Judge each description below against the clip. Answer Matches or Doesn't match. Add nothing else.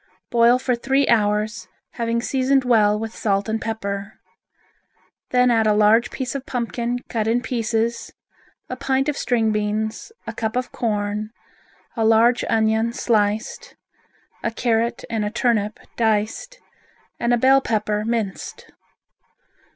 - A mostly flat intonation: Matches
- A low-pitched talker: Doesn't match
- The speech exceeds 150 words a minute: Doesn't match